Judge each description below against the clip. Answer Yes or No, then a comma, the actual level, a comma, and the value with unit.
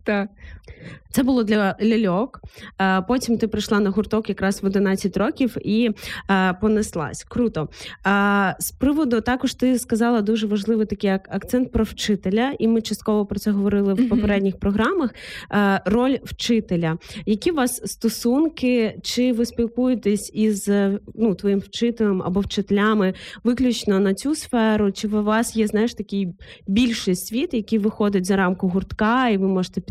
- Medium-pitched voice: No, high, 215 Hz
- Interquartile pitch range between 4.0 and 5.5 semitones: No, average, 2.9 semitones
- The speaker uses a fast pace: No, average, 145 wpm